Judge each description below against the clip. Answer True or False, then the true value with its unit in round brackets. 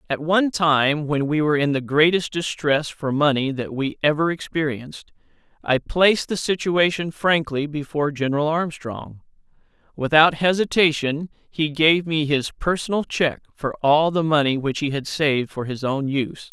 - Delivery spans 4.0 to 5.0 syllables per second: True (4.8 syllables/s)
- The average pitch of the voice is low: False (150 Hz)